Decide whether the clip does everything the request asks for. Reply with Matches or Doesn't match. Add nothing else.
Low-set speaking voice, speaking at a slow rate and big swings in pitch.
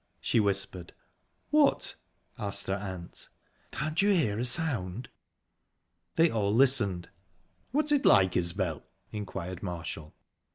Matches